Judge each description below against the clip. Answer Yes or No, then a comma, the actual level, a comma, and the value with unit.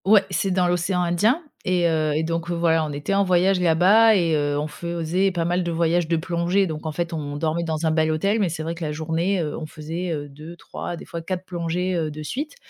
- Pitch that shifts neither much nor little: No, narrow, 2.3 semitones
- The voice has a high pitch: No, medium, 170 Hz